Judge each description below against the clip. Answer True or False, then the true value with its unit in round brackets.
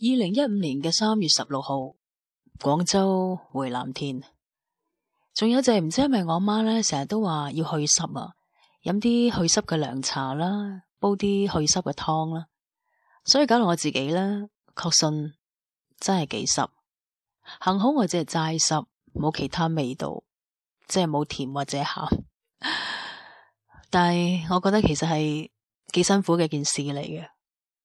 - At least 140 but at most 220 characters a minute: True (215 characters per minute)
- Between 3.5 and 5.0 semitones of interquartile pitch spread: False (5.4 semitones)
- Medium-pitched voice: True (170 Hz)